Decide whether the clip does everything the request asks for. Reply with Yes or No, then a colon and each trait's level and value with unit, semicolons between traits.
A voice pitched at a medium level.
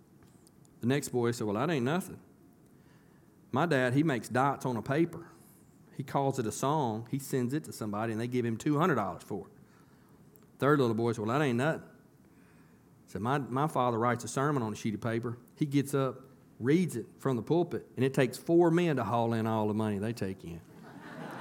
No: low, 125 Hz